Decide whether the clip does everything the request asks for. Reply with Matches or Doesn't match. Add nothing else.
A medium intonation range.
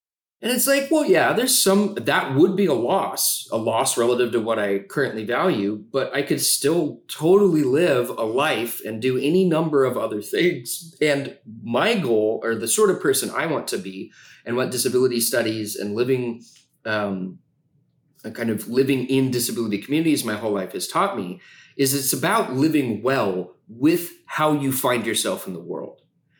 Doesn't match